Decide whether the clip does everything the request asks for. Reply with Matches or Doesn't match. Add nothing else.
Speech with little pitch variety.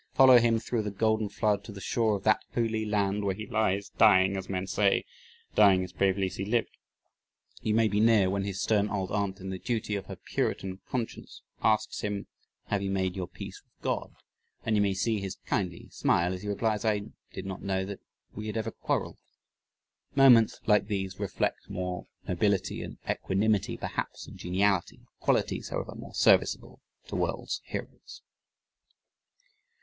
Matches